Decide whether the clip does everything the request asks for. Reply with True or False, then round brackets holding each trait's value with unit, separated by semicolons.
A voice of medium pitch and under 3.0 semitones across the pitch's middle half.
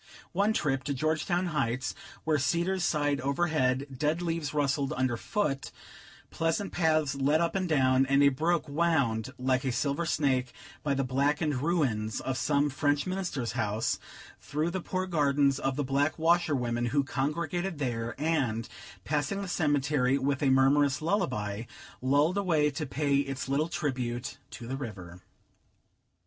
False (145 Hz; 3.5 semitones)